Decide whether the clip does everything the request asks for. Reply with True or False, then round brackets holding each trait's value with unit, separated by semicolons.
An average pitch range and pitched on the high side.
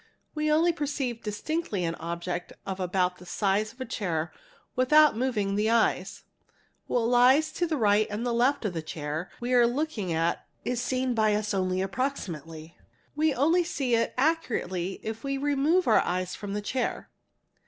False (6.6 semitones; 225 Hz)